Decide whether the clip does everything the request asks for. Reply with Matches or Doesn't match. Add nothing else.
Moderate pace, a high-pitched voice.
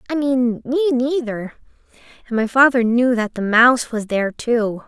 Matches